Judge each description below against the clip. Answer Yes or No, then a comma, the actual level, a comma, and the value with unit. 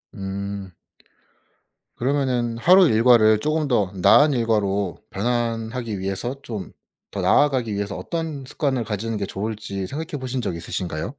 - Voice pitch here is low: Yes, low, 115 Hz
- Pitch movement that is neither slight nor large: Yes, average, 4.7 semitones